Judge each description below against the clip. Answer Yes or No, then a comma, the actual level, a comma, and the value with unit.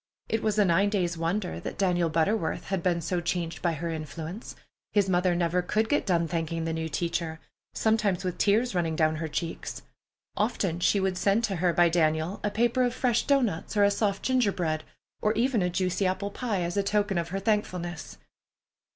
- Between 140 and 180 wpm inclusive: No, average, 200 wpm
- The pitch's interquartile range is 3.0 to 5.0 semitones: Yes, average, 3.7 semitones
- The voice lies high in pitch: No, medium, 180 Hz